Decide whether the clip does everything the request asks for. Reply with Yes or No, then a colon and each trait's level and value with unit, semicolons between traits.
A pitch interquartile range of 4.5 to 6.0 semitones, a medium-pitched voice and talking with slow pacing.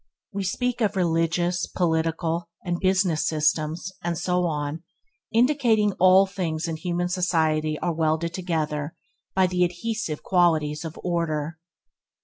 No: average, 2.7 semitones; medium, 170 Hz; slow, 130 wpm